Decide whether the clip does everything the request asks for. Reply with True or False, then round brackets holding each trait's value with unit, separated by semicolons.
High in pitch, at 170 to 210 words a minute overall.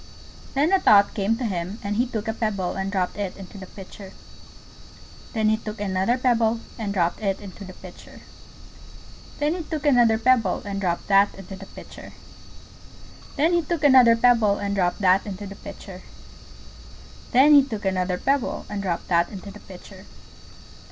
True (205 Hz; 175 wpm)